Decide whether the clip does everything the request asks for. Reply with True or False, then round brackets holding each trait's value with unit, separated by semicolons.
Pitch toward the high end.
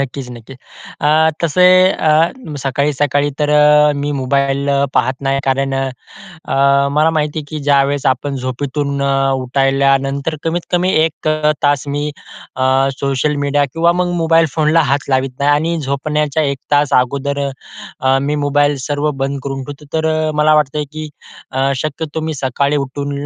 False (145 Hz)